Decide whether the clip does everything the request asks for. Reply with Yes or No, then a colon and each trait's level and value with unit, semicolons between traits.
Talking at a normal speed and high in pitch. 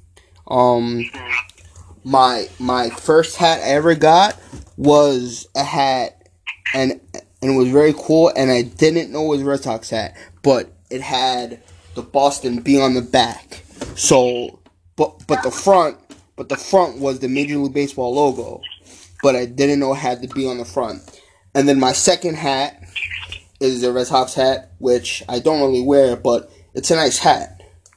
No: average, 175 wpm; low, 130 Hz